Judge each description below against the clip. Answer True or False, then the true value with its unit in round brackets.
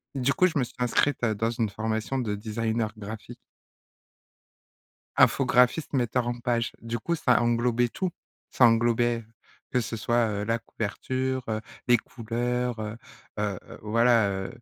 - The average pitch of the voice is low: True (115 Hz)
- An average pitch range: False (2.0 semitones)